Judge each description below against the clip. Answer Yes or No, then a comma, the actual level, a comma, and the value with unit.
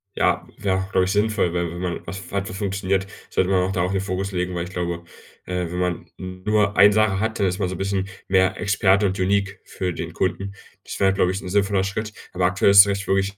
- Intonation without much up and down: Yes, narrow, 1.4 semitones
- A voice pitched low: Yes, very low, 95 Hz